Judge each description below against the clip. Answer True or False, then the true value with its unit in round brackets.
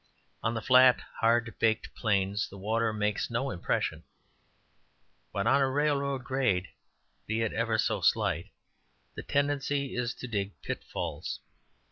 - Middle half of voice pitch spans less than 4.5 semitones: True (3.6 semitones)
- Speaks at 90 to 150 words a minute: True (135 wpm)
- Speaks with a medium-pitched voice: False (115 Hz)